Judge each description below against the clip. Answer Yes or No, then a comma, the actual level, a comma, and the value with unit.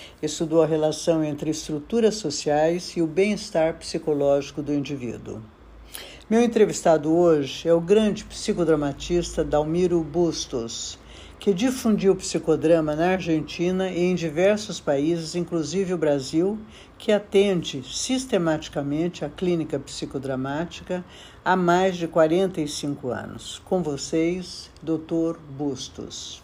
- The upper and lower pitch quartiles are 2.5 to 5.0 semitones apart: Yes, average, 3.5 semitones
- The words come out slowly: Yes, slow, 110 wpm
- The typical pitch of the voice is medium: Yes, medium, 165 Hz